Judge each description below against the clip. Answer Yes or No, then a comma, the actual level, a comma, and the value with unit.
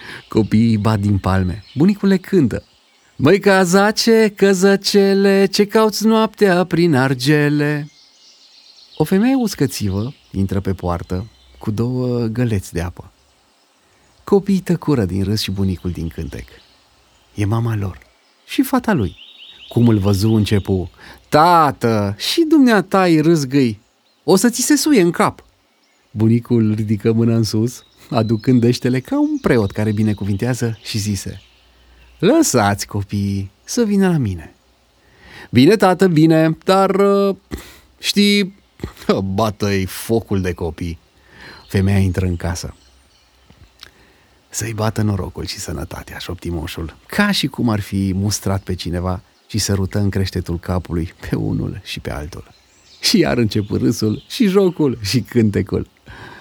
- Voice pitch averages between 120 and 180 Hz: No, low, 110 Hz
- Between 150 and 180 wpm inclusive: No, average, 130 wpm